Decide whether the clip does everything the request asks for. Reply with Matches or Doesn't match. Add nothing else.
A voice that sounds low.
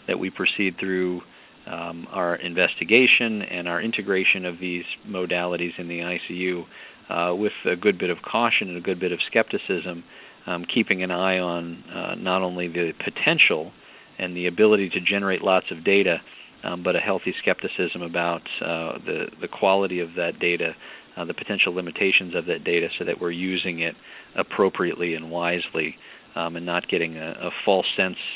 Matches